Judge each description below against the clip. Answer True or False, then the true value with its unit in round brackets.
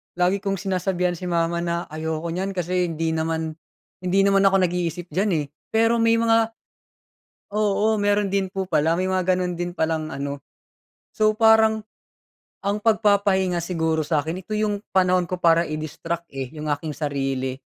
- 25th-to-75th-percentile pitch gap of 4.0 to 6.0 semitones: False (3.5 semitones)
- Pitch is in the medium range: True (180 Hz)